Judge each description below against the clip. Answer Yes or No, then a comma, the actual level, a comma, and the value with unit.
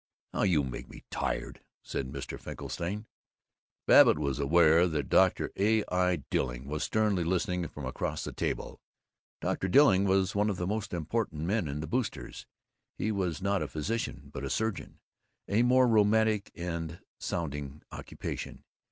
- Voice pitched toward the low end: Yes, very low, 90 Hz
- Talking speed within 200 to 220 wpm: No, average, 155 wpm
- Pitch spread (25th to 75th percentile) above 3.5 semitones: Yes, wide, 5.4 semitones